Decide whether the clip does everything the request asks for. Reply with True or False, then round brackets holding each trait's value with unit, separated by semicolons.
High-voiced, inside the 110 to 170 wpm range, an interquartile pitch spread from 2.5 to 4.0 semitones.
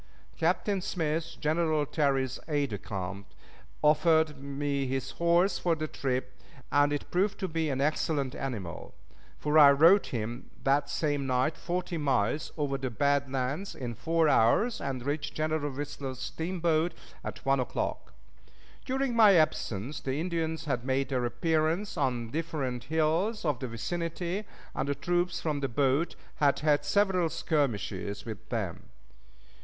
False (145 Hz; 150 wpm; 3.7 semitones)